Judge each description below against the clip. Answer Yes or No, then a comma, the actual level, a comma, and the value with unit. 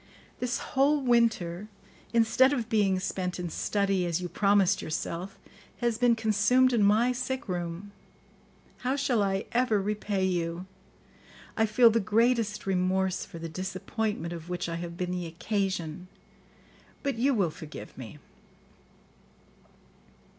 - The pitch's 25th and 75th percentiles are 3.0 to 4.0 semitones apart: No, average, 4.5 semitones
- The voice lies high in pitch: Yes, high, 200 Hz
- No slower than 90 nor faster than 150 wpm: Yes, slow, 135 wpm